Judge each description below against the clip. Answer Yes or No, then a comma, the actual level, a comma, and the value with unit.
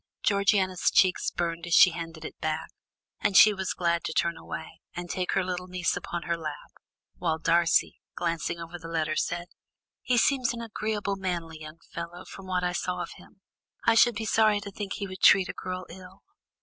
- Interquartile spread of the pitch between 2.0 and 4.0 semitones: Yes, average, 2.8 semitones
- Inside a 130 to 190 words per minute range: No, average, 200 wpm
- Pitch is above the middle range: No, medium, 180 Hz